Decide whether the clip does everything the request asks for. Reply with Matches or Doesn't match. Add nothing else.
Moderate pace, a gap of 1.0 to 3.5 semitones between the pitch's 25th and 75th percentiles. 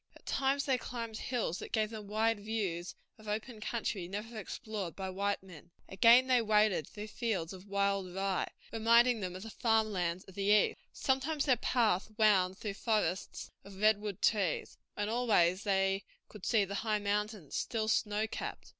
Matches